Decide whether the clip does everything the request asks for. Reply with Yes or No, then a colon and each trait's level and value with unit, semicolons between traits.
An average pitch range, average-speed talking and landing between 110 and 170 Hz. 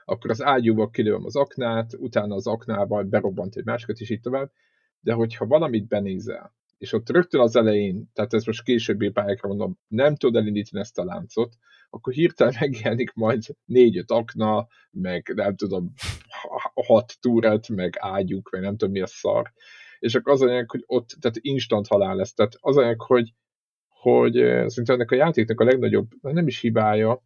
No: average, 3.4 semitones; fast, 170 wpm; low, 115 Hz